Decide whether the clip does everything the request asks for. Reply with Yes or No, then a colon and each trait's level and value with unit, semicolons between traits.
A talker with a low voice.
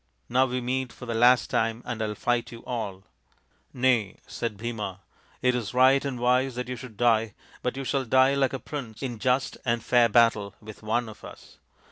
Yes: low, 120 Hz